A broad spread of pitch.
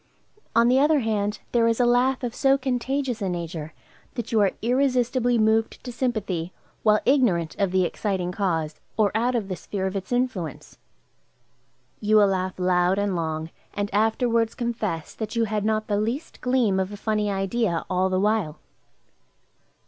No: average, 4.2 semitones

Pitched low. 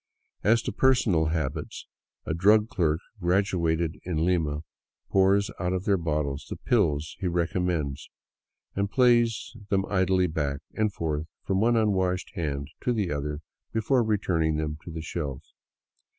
Yes: very low, 90 Hz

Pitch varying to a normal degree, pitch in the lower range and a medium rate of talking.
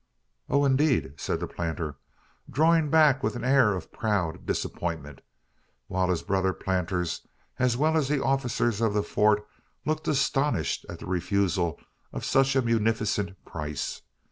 No: wide, 6.9 semitones; low, 105 Hz; average, 145 wpm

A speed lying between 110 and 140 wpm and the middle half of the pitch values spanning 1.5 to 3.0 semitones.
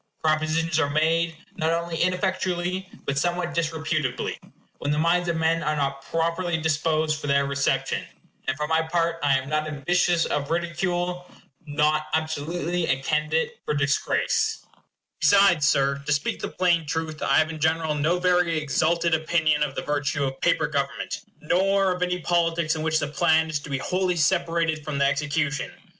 No: average, 170 wpm; narrow, 2.4 semitones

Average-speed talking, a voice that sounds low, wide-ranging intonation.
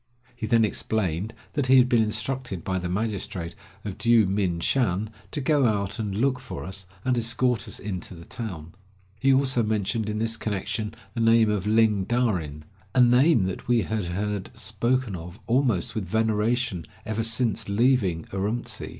No: average, 175 wpm; low, 110 Hz; average, 3.9 semitones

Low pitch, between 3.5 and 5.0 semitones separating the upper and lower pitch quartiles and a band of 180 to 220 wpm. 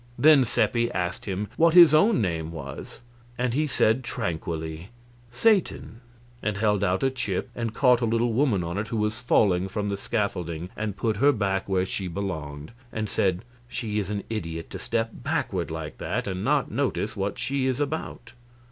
Yes: low, 105 Hz; average, 4.7 semitones; average, 185 wpm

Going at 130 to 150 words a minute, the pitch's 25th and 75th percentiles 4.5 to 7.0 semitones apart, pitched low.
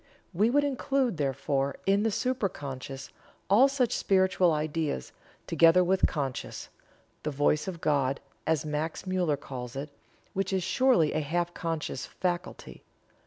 No: average, 140 wpm; average, 5.0 semitones; medium, 165 Hz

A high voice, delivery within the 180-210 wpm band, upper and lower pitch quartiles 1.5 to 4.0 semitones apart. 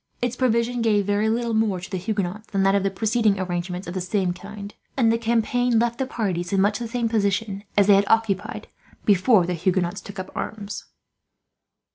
Yes: high, 205 Hz; average, 200 wpm; average, 3.0 semitones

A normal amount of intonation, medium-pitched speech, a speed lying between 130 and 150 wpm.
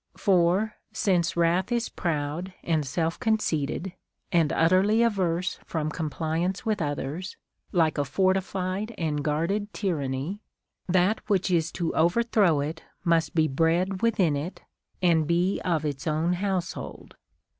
Yes: average, 3.3 semitones; medium, 175 Hz; slow, 135 wpm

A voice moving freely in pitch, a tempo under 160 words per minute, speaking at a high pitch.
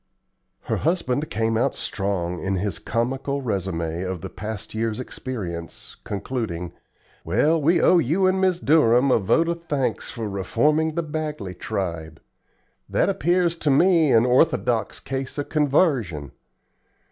No: wide, 8.0 semitones; average, 140 wpm; low, 125 Hz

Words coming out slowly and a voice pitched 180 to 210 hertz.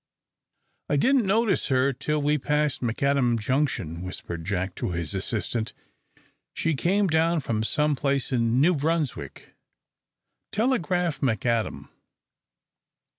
No: slow, 115 wpm; medium, 140 Hz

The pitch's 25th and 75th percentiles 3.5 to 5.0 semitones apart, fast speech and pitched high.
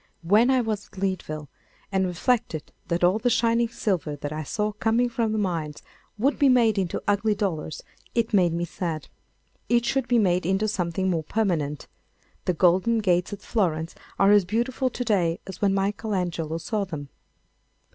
No: average, 4.6 semitones; average, 175 wpm; high, 195 Hz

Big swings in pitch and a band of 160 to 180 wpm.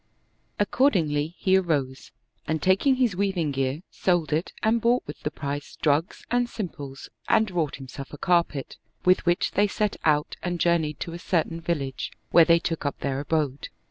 No: average, 4.3 semitones; average, 175 wpm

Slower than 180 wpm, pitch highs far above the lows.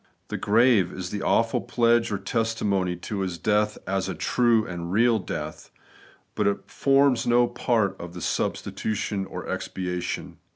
No: average, 155 wpm; average, 3.8 semitones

